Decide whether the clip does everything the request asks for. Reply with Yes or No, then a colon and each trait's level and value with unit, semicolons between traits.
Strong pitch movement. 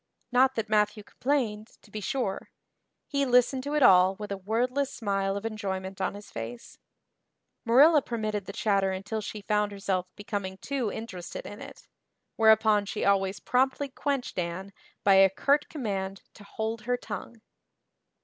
No: average, 4.0 semitones